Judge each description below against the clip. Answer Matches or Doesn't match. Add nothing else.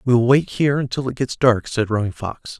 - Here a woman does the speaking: Doesn't match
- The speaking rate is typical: Doesn't match